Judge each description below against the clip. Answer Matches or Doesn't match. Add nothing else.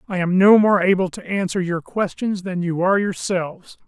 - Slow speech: Doesn't match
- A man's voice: Matches